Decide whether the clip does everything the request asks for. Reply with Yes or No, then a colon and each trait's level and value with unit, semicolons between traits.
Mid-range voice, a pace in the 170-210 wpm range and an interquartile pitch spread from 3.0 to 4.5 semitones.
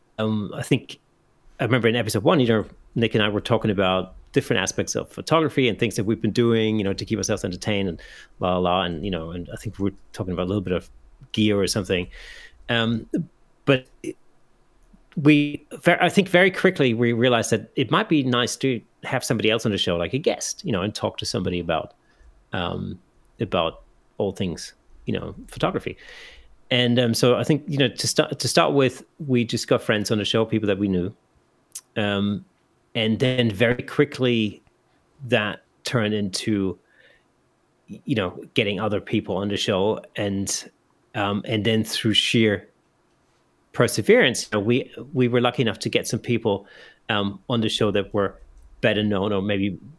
No: low, 110 Hz; average, 190 wpm; average, 3.9 semitones